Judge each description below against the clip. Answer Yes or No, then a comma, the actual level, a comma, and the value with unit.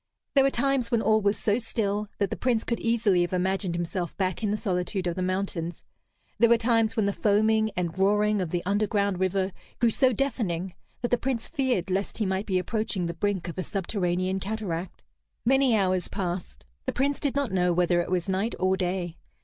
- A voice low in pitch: No, high, 200 Hz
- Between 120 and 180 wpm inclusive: No, fast, 205 wpm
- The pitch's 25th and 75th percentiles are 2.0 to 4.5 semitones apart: Yes, average, 3.6 semitones